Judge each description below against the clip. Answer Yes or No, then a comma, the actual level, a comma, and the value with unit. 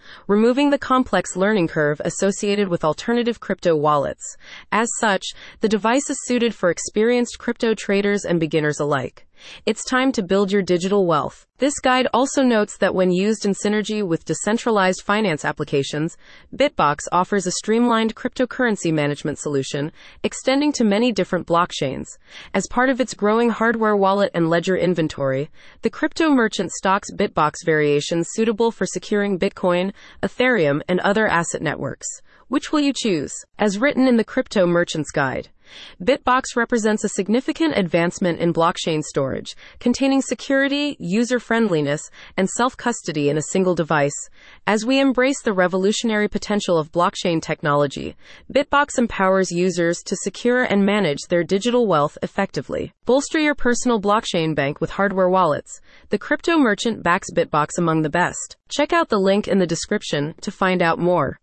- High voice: Yes, high, 200 Hz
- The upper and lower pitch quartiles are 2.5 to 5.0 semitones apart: No, wide, 5.6 semitones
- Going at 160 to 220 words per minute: No, average, 150 wpm